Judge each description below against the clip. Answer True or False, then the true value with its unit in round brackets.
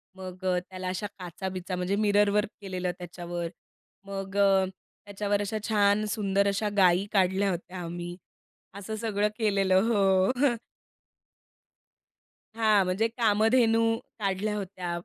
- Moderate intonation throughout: False (2.2 semitones)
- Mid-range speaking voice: False (195 Hz)